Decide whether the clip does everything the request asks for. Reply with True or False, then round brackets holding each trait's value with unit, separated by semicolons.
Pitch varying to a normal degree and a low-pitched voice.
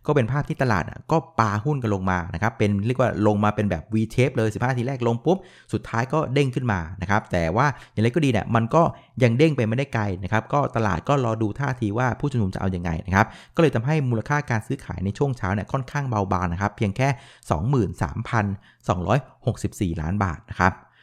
True (5.0 semitones; 115 Hz)